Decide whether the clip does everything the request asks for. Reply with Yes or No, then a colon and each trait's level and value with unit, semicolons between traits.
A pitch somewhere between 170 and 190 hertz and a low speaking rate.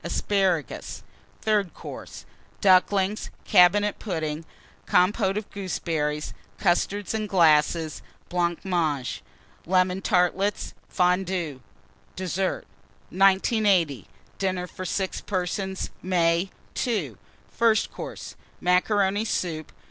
Yes: medium, 185 Hz; slow, 85 wpm